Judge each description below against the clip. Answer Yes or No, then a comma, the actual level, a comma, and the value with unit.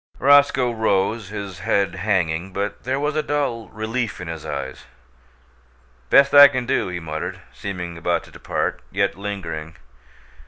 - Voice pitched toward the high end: No, low, 100 Hz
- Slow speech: No, average, 150 wpm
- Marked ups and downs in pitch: Yes, wide, 6.1 semitones